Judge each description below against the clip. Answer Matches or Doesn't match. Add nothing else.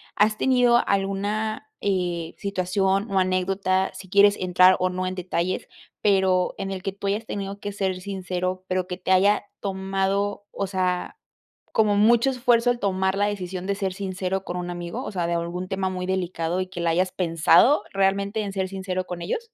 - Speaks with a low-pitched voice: Doesn't match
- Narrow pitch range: Matches